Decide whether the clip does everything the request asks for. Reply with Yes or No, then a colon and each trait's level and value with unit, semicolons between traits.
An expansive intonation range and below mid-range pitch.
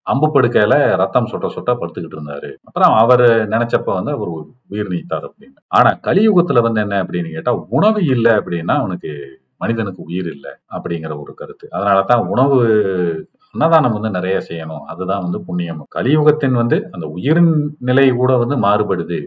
Yes: wide, 7.0 semitones; low, 110 Hz